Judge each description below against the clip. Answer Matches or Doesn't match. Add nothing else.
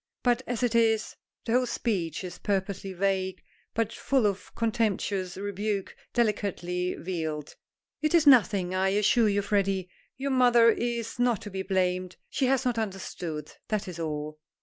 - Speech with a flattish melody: Doesn't match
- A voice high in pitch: Matches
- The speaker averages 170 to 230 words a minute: Doesn't match